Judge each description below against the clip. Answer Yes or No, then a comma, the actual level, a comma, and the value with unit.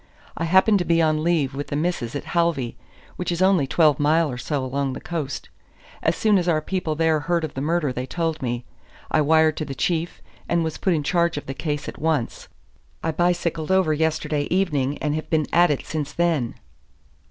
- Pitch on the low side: No, medium, 160 Hz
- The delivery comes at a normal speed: No, fast, 210 wpm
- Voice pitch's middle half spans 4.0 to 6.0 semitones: No, average, 2.9 semitones